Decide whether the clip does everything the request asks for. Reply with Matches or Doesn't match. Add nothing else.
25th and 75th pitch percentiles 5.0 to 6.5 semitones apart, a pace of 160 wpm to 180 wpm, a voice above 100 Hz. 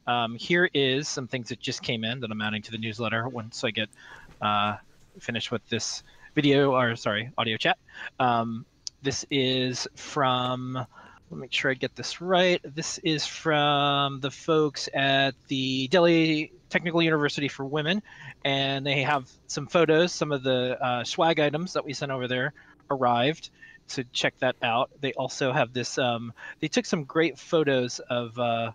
Doesn't match